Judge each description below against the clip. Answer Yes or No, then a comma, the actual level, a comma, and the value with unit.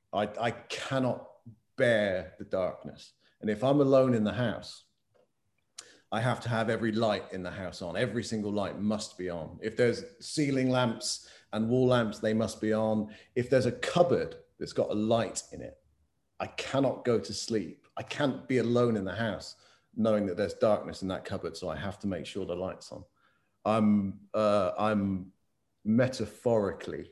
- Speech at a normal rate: Yes, average, 180 wpm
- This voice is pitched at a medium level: No, low, 110 Hz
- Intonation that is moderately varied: Yes, average, 3.3 semitones